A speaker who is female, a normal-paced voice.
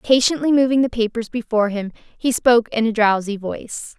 Yes: female; average, 180 wpm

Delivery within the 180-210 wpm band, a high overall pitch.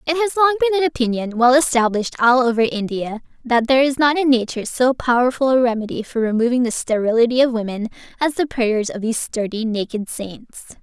Yes: average, 195 wpm; high, 245 Hz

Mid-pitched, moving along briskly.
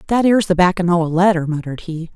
Yes: medium, 175 Hz; fast, 250 wpm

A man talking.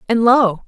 No: female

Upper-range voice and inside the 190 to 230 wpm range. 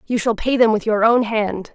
No: high, 220 Hz; fast, 275 wpm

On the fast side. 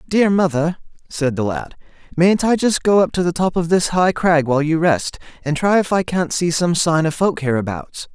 Yes: fast, 230 wpm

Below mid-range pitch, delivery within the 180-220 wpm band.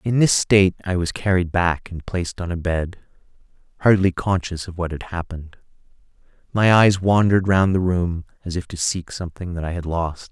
Yes: very low, 90 Hz; average, 190 wpm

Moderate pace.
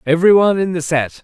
Yes: average, 195 wpm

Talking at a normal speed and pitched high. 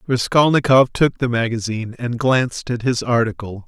No: average, 145 wpm; low, 120 Hz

